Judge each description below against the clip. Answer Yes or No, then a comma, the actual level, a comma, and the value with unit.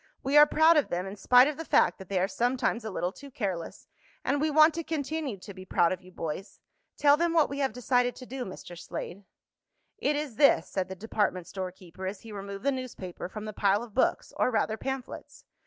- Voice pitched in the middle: No, high, 225 Hz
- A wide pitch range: Yes, wide, 6.8 semitones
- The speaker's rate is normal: No, fast, 230 wpm